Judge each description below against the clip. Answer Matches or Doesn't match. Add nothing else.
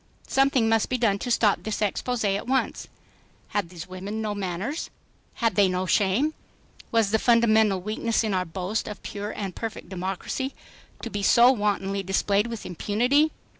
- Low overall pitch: Doesn't match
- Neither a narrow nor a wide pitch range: Matches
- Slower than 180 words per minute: Matches